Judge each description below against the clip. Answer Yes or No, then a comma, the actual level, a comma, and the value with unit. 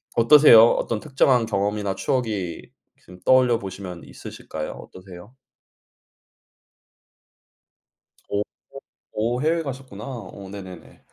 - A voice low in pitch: Yes, low, 105 Hz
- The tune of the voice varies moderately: Yes, average, 5.0 semitones